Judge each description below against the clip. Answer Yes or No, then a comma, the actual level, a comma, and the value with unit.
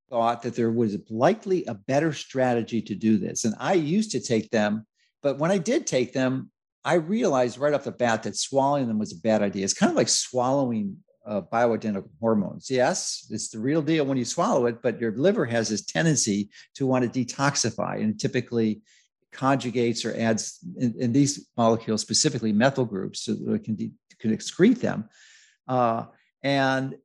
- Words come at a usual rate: Yes, average, 190 wpm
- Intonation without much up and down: No, average, 4.1 semitones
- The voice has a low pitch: Yes, low, 125 Hz